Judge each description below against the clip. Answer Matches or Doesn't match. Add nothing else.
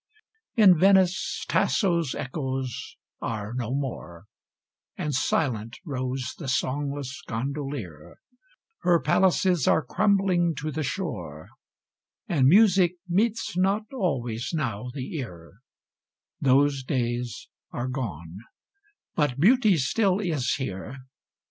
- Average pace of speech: Doesn't match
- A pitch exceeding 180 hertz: Doesn't match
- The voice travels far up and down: Matches